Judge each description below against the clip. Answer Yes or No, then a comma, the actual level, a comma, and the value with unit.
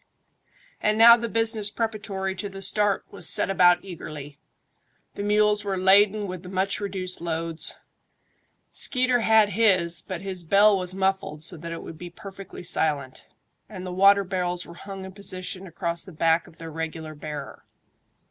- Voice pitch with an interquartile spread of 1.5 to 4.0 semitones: Yes, average, 3.1 semitones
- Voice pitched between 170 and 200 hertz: Yes, high, 190 Hz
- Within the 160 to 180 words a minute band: Yes, average, 165 wpm